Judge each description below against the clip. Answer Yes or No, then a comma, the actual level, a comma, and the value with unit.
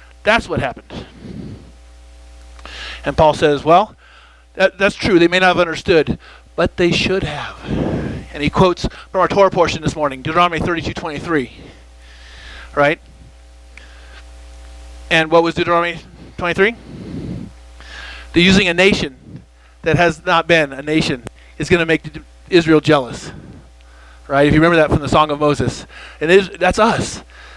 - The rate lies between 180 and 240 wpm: No, average, 150 wpm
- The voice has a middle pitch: Yes, medium, 150 Hz